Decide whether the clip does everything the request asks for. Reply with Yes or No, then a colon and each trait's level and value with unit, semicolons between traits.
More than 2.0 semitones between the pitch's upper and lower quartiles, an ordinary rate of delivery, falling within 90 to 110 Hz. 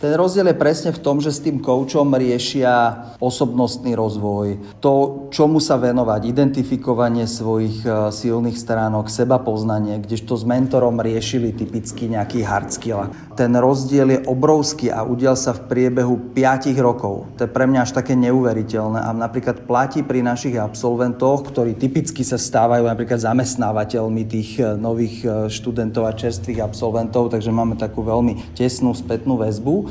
No: narrow, 2.5 semitones; average, 150 wpm; low, 120 Hz